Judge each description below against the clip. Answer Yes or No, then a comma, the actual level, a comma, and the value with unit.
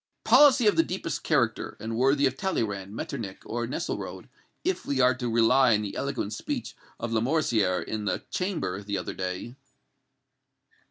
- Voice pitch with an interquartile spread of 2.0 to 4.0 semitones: No, average, 5.0 semitones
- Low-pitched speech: Yes, low, 120 Hz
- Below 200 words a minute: Yes, average, 160 wpm